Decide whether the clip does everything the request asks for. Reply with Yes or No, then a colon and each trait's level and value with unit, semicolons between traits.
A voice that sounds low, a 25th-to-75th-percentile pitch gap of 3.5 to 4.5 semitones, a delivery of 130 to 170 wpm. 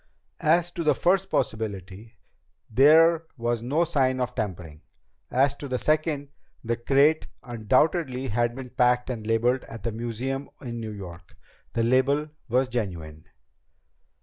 Yes: low, 125 Hz; average, 4.0 semitones; average, 140 wpm